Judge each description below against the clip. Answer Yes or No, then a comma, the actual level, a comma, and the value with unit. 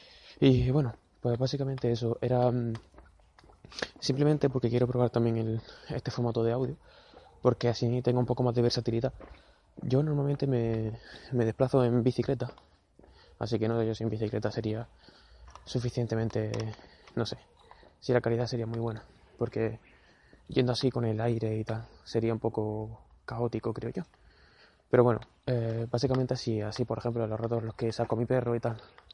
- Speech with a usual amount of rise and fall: No, narrow, 1.7 semitones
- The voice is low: Yes, low, 120 Hz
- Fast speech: No, average, 170 wpm